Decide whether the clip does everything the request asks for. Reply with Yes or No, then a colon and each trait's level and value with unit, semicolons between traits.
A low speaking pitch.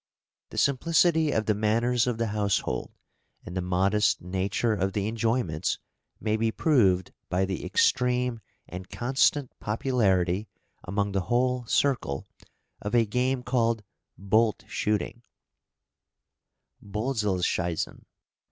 Yes: low, 110 Hz